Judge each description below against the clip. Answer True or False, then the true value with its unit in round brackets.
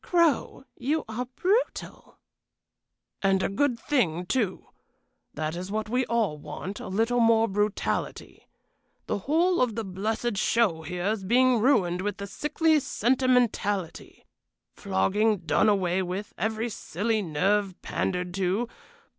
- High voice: True (210 Hz)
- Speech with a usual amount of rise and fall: True (4.5 semitones)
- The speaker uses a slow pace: True (130 wpm)